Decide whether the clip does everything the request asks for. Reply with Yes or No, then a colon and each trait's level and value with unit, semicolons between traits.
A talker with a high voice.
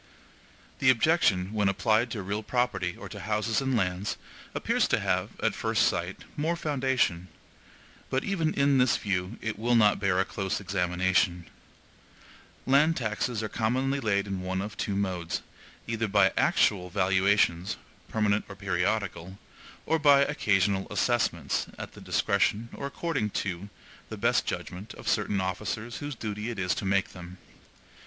No: low, 105 Hz